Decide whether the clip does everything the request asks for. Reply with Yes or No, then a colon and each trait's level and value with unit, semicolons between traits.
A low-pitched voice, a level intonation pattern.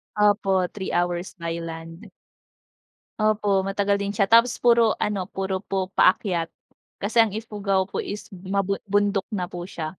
No: high, 195 Hz; narrow, 2.2 semitones